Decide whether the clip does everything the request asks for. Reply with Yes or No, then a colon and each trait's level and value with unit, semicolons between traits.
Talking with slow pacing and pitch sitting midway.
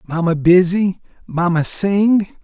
Yes: slow, 100 wpm; medium, 180 Hz